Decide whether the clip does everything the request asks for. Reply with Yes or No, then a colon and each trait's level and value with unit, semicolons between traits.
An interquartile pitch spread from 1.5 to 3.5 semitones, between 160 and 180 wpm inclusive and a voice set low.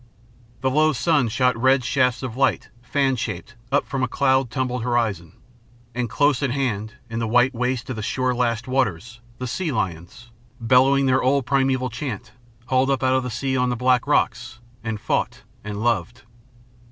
Yes: narrow, 2.4 semitones; average, 175 wpm; low, 125 Hz